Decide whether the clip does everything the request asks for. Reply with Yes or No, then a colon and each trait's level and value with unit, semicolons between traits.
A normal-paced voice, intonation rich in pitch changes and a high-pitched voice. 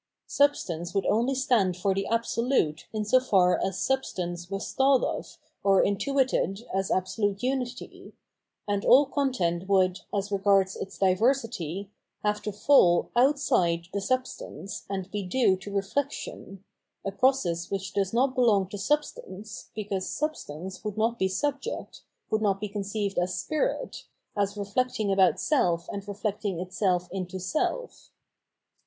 No: average, 150 wpm; average, 4.7 semitones; high, 200 Hz